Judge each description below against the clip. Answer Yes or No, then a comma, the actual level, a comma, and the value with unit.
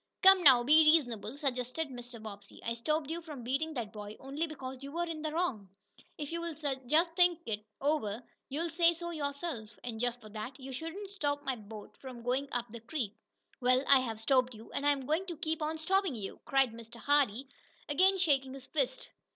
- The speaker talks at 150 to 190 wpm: No, average, 200 wpm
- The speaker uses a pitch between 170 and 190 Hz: No, very high, 275 Hz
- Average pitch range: Yes, average, 4.8 semitones